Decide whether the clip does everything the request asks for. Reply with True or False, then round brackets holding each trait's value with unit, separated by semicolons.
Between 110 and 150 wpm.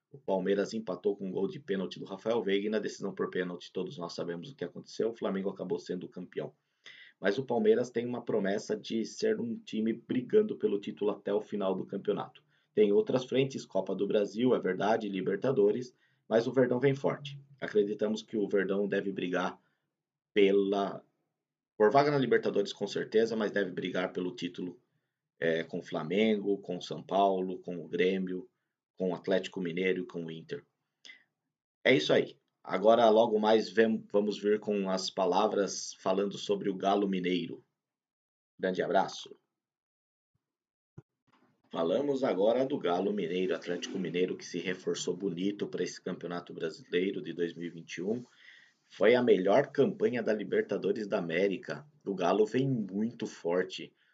False (160 wpm)